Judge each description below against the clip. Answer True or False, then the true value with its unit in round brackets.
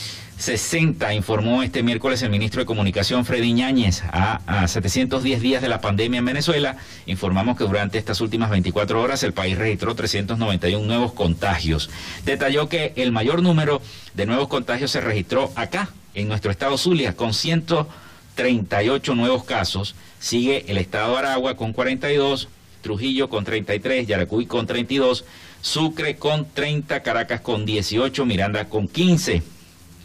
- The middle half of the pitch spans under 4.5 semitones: False (5.6 semitones)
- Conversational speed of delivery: True (145 wpm)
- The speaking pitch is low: True (110 Hz)